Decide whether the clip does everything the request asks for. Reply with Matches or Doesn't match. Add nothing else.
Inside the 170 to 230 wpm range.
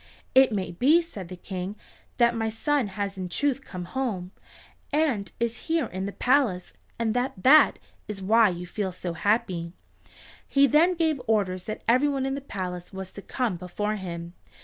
Matches